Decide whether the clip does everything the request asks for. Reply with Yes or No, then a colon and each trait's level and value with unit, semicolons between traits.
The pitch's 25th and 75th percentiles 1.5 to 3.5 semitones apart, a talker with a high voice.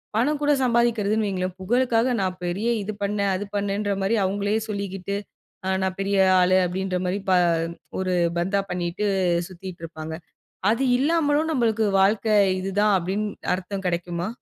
Yes: average, 3.0 semitones; high, 200 Hz